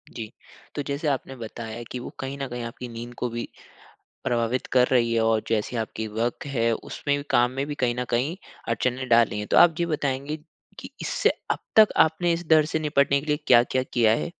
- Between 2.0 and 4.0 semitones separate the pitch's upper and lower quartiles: Yes, average, 3.4 semitones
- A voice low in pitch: Yes, low, 125 Hz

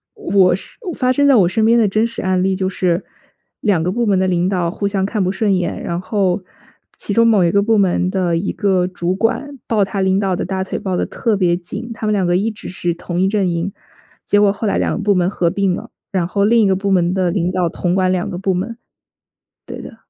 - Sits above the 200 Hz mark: No, high, 190 Hz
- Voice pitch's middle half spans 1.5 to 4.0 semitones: Yes, narrow, 2.4 semitones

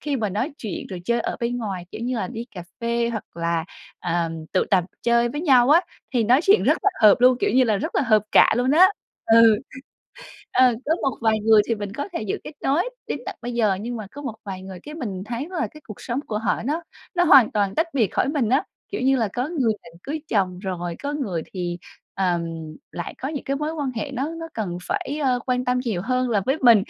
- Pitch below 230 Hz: No, high, 235 Hz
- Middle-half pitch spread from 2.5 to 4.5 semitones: No, average, 5.2 semitones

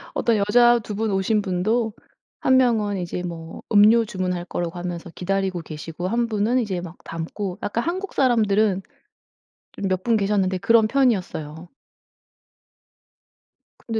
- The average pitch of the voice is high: Yes, high, 200 Hz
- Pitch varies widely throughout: No, average, 4.1 semitones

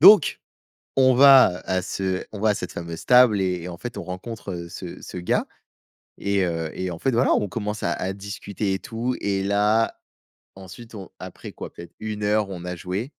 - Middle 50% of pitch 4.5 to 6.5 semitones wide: No, average, 3.6 semitones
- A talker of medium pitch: No, low, 100 Hz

